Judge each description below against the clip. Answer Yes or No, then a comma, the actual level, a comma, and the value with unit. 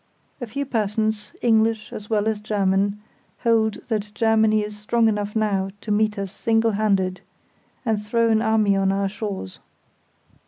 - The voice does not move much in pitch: Yes, narrow, 1.5 semitones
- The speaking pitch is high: Yes, high, 215 Hz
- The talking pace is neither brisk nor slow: Yes, average, 155 wpm